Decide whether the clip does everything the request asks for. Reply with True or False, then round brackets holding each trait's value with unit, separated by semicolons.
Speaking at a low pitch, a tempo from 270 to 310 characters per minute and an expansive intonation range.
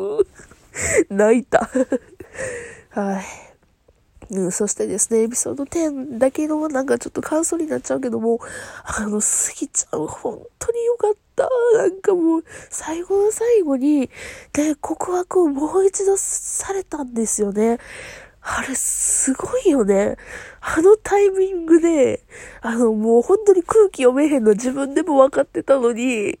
False (310 Hz; 275 characters per minute; 8.7 semitones)